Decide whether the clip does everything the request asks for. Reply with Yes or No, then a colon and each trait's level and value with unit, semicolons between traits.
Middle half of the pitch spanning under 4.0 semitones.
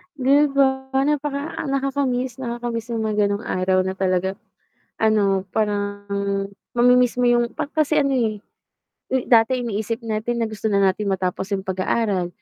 No: average, 4.3 semitones